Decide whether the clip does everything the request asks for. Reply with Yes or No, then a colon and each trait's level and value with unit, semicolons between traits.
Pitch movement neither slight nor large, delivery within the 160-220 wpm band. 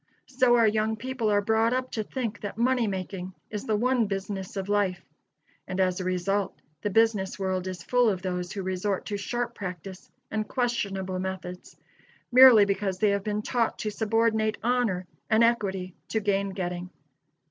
Yes: average, 3.2 semitones; average, 175 wpm